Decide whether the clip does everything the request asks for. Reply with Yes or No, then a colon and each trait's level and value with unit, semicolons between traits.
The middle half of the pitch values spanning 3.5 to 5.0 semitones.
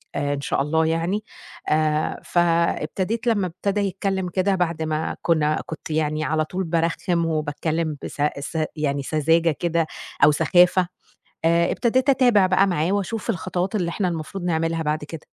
No: average, 3.1 semitones